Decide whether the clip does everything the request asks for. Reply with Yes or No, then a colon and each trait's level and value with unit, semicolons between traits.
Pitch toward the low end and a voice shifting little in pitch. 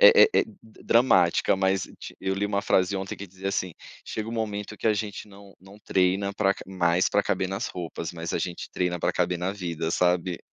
Yes: very low, 95 Hz; narrow, 2.3 semitones